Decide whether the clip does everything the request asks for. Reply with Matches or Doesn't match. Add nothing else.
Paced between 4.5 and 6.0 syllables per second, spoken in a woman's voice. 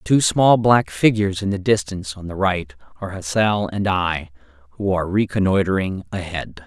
Doesn't match